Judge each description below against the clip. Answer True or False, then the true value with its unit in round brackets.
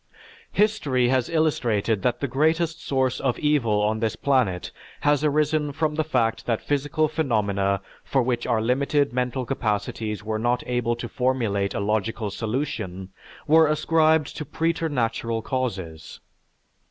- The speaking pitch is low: True (125 Hz)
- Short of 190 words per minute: True (140 wpm)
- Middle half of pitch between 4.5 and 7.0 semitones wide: True (5.1 semitones)